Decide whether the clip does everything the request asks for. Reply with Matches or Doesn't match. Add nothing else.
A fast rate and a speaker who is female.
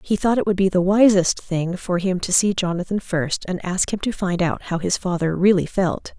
Matches